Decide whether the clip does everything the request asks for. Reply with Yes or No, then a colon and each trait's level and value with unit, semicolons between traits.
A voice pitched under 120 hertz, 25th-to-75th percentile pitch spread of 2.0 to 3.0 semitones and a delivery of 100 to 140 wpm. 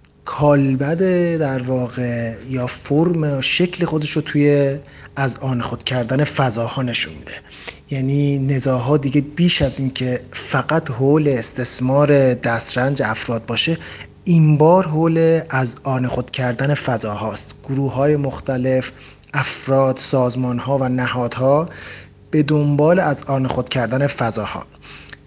No: low, 135 Hz; average, 2.7 semitones; average, 125 wpm